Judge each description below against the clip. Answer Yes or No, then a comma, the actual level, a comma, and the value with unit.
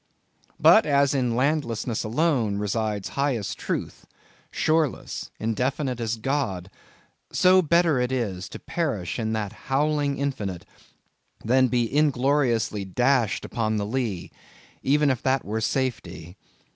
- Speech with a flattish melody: No, average, 4.6 semitones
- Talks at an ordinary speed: No, slow, 120 wpm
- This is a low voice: Yes, low, 125 Hz